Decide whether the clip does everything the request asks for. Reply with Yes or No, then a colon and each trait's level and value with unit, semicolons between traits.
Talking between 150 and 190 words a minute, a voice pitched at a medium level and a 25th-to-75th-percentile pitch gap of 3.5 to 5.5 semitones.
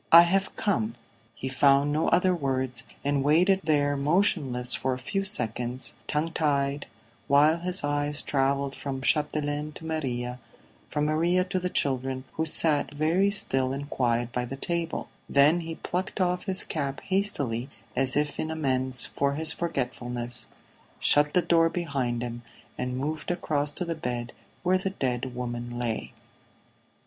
Yes: average, 155 wpm; medium, 145 Hz; average, 4.2 semitones